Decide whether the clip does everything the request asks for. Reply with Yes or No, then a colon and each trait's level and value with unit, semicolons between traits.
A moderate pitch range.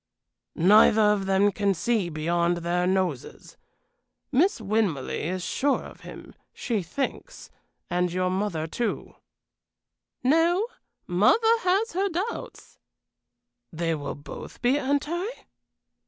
No: wide, 8.6 semitones